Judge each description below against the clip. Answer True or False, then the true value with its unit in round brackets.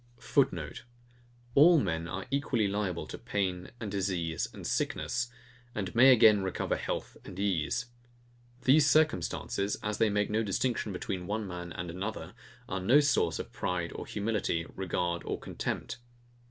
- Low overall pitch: True (100 Hz)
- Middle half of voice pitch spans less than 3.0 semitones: False (4.4 semitones)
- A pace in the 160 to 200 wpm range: False (150 wpm)